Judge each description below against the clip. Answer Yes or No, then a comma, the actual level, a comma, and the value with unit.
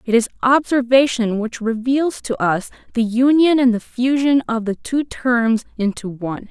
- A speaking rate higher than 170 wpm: No, average, 165 wpm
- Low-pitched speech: No, high, 240 Hz